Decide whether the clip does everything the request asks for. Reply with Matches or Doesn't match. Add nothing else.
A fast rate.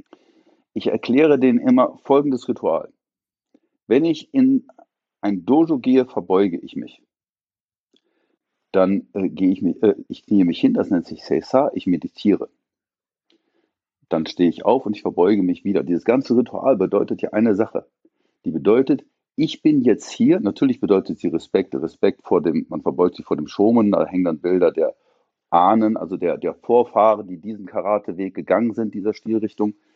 Doesn't match